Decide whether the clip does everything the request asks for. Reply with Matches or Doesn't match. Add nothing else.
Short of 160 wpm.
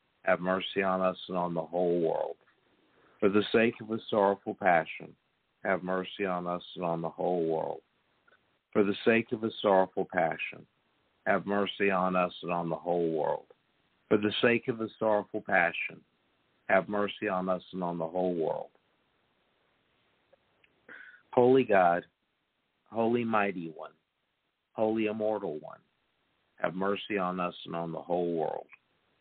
Matches